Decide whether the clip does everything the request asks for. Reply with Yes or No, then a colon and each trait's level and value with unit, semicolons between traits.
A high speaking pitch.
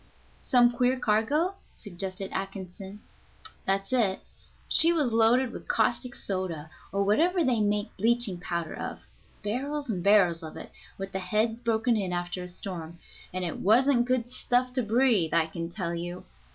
Yes: high, 210 Hz